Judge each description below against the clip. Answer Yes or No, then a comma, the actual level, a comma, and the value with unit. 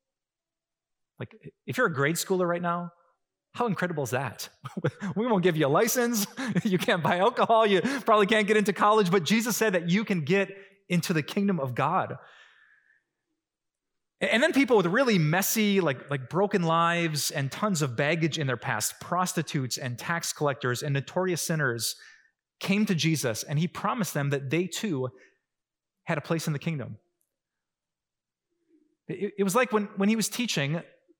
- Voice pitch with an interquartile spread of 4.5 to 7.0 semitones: Yes, wide, 5.5 semitones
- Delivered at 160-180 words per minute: Yes, average, 170 wpm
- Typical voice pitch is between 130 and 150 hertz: No, medium, 180 Hz